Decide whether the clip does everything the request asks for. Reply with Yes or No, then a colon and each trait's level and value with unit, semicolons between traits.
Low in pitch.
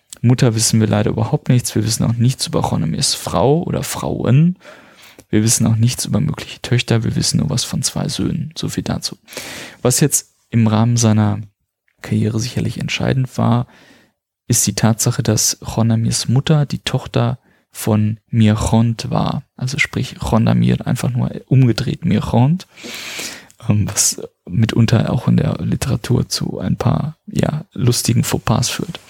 Yes: low, 120 Hz